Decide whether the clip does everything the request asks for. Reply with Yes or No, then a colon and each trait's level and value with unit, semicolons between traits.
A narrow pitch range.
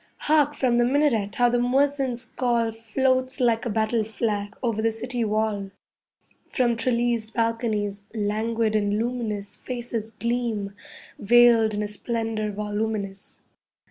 Yes: narrow, 2.3 semitones